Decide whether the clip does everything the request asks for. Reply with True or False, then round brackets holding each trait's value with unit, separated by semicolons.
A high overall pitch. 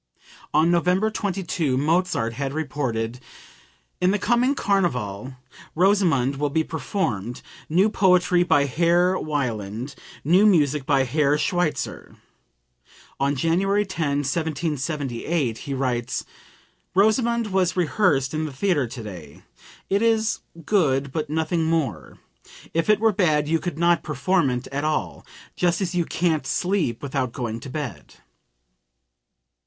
False (155 Hz)